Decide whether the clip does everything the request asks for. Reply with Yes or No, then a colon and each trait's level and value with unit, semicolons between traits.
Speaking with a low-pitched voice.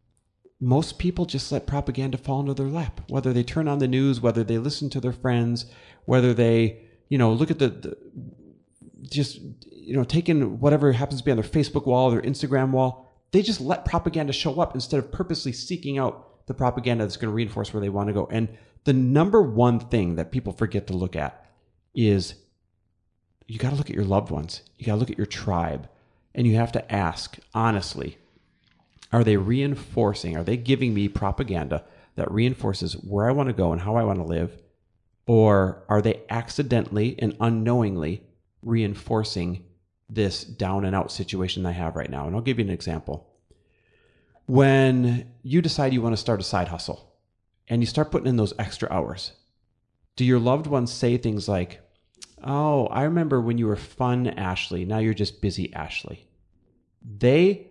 Yes: low, 115 Hz